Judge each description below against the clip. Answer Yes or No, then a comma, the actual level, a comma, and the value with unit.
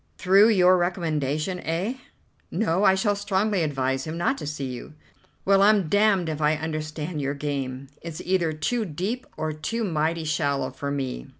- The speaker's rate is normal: Yes, average, 170 wpm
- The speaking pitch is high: No, medium, 160 Hz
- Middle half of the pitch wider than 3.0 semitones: Yes, average, 4.4 semitones